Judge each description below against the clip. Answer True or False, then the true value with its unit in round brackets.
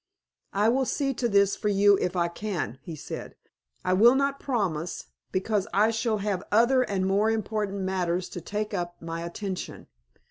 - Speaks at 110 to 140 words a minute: False (175 wpm)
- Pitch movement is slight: False (3.4 semitones)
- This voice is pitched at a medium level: False (200 Hz)